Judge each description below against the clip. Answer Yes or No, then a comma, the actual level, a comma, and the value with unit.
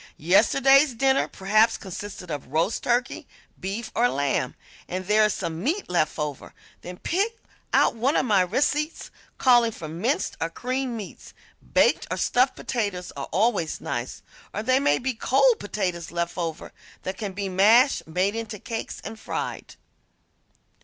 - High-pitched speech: Yes, high, 210 Hz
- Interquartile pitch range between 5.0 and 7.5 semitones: Yes, wide, 5.6 semitones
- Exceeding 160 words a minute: No, average, 155 wpm